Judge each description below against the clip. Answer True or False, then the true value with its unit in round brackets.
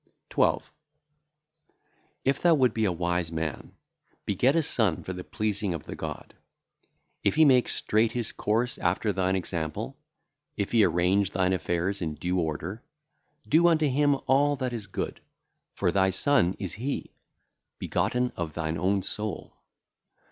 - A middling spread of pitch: False (5.9 semitones)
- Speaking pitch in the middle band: False (100 Hz)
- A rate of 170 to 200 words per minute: False (150 wpm)